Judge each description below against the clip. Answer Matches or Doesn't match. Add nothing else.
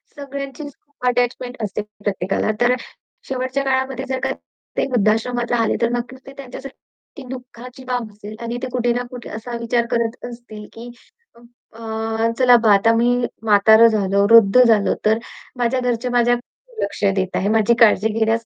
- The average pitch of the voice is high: Matches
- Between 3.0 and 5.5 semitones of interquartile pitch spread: Doesn't match